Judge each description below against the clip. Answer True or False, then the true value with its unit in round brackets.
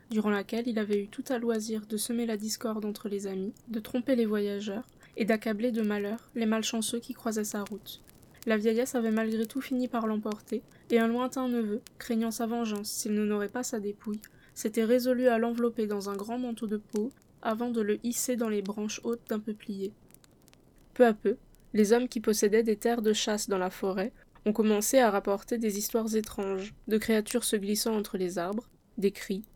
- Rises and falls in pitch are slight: True (2.1 semitones)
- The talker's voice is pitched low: False (220 Hz)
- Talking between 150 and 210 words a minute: True (205 wpm)